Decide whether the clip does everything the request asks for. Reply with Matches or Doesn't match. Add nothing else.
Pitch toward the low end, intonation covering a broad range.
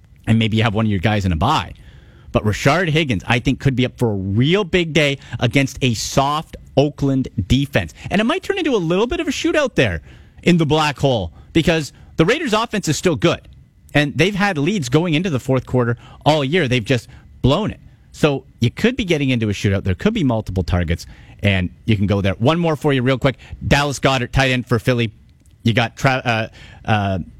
Matches